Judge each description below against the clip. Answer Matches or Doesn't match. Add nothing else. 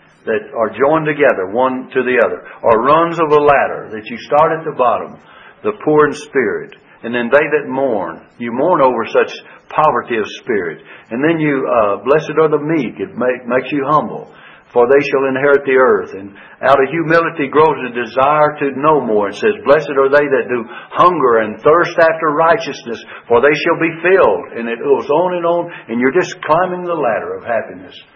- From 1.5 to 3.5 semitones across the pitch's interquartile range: Doesn't match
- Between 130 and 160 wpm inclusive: Doesn't match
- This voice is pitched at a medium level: Matches